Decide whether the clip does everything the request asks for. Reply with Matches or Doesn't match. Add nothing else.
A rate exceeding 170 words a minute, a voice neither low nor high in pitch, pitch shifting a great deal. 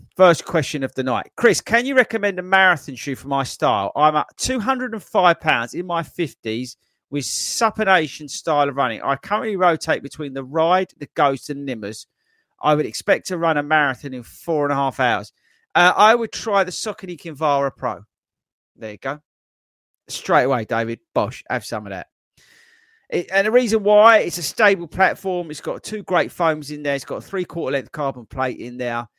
Matches